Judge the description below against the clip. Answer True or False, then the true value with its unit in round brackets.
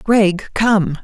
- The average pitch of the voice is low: False (200 Hz)